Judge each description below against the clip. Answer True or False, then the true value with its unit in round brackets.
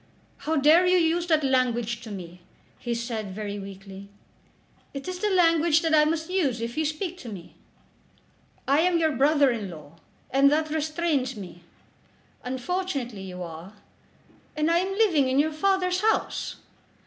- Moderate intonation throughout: False (7.0 semitones)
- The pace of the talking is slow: False (160 wpm)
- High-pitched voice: True (285 Hz)